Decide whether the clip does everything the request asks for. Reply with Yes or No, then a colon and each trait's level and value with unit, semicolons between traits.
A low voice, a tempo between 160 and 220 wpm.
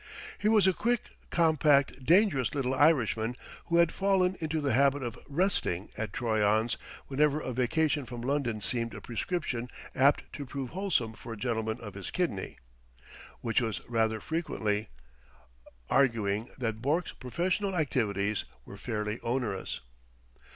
No: low, 130 Hz; average, 140 wpm